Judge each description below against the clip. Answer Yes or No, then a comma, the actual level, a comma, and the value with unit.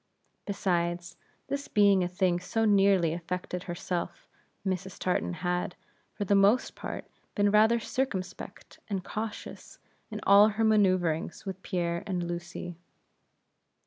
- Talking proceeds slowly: Yes, slow, 125 wpm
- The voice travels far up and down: No, narrow, 2.6 semitones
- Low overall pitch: No, medium, 185 Hz